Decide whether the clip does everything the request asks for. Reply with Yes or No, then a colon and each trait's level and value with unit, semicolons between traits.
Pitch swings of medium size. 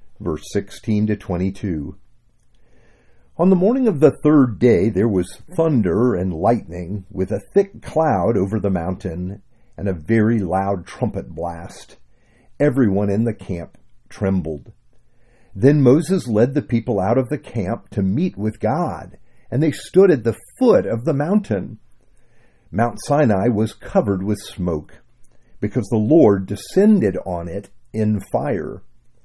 Yes: average, 4.7 semitones